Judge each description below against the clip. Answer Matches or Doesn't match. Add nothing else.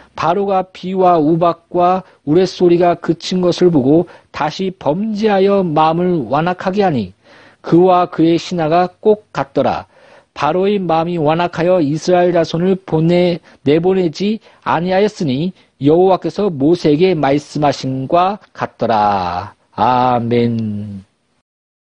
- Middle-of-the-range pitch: Matches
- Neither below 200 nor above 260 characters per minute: Matches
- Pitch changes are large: Doesn't match